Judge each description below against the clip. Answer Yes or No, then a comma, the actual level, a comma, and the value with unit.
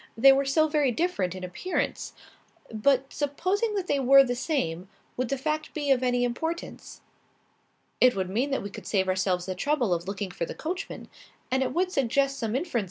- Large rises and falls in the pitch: Yes, wide, 7.4 semitones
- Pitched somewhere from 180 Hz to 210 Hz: No, very high, 260 Hz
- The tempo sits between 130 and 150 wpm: No, average, 165 wpm